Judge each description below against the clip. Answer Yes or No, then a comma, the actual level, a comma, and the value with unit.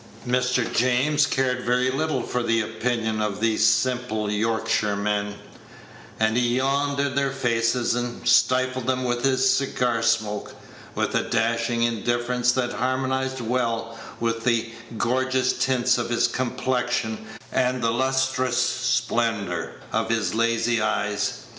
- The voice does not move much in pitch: Yes, narrow, 2.1 semitones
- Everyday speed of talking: No, slow, 130 wpm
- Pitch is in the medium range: No, low, 120 Hz